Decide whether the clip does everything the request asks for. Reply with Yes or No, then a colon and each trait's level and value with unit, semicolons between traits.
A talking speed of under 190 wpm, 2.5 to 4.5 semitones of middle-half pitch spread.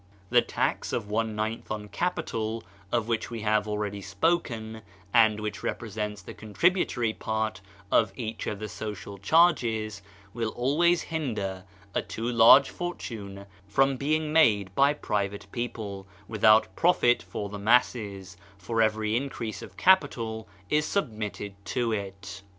Yes: average, 140 wpm; average, 2.9 semitones